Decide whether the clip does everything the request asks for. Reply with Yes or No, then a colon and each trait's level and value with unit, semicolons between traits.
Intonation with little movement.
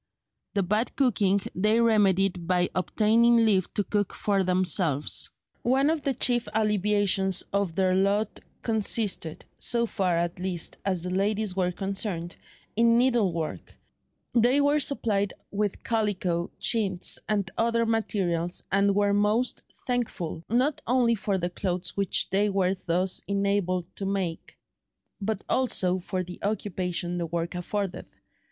No: average, 3.3 semitones